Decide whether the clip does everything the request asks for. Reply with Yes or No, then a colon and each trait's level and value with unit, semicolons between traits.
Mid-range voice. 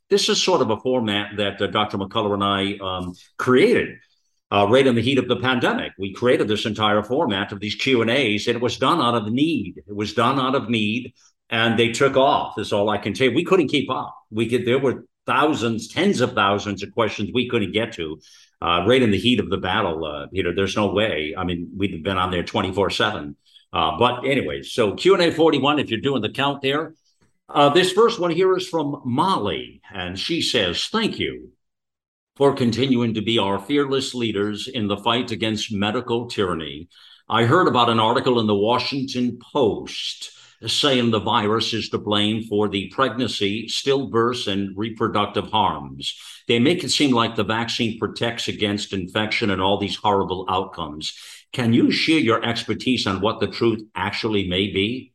No: low, 110 Hz